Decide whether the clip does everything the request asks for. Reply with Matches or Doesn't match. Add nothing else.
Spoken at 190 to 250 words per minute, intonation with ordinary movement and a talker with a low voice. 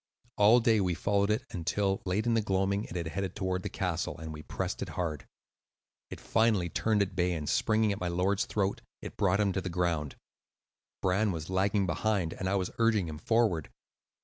Matches